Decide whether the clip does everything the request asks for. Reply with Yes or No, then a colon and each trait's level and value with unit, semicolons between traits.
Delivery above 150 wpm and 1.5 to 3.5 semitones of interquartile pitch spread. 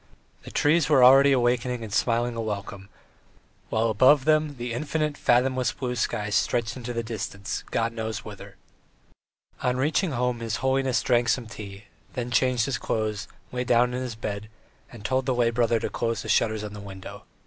Yes: average, 180 wpm; narrow, 2.6 semitones